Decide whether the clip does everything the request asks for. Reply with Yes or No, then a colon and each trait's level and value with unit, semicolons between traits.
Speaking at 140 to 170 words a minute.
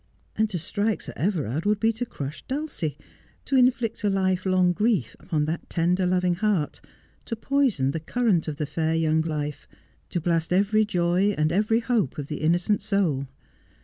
No: average, 180 wpm